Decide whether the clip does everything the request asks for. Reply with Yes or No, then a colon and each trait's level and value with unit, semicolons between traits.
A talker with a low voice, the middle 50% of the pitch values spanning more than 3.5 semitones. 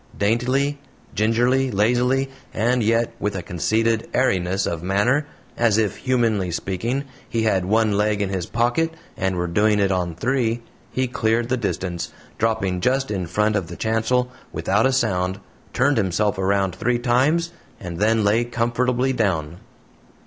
Yes: low, 110 Hz; average, 4.3 semitones